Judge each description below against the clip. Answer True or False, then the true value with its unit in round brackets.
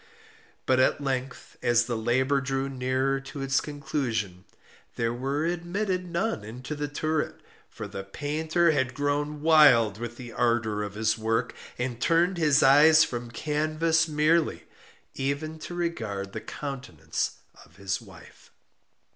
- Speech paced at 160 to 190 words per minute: False (140 wpm)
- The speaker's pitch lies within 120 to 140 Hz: True (135 Hz)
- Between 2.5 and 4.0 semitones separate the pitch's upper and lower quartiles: False (4.7 semitones)